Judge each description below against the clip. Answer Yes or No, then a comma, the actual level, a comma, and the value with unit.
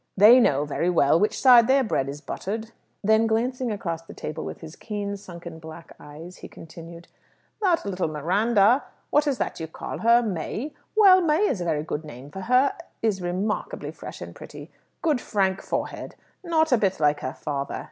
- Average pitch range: No, wide, 6.9 semitones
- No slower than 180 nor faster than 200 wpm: Yes, average, 190 wpm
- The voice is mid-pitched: No, high, 200 Hz